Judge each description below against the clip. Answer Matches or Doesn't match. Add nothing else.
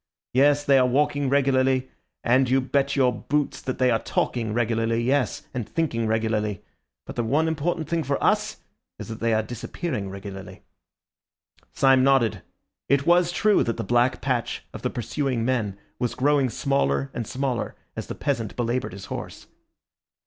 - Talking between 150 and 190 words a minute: Matches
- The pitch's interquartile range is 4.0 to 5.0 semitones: Doesn't match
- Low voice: Matches